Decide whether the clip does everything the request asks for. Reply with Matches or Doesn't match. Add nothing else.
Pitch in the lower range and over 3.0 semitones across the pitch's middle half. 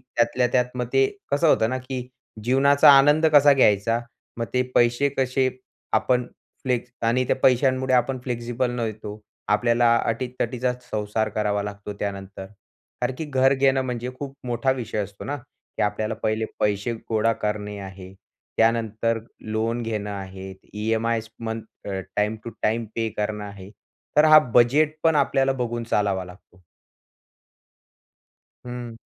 Matches